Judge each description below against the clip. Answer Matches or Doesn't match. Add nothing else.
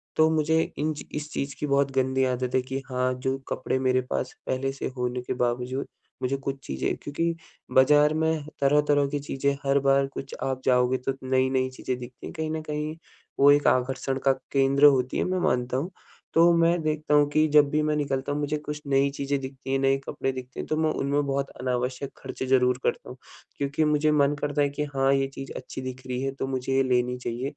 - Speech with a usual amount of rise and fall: Doesn't match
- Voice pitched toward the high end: Doesn't match